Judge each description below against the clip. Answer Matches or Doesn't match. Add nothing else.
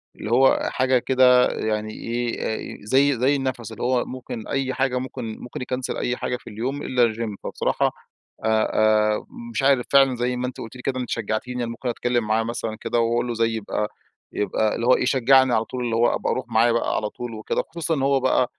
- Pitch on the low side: Matches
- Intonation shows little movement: Matches